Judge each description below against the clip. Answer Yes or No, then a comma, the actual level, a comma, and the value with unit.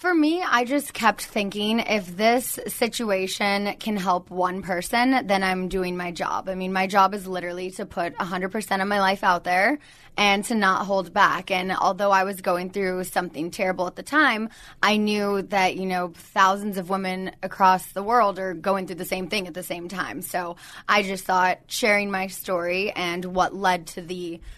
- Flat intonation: Yes, narrow, 2.0 semitones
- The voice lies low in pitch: No, high, 190 Hz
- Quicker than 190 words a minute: Yes, average, 200 wpm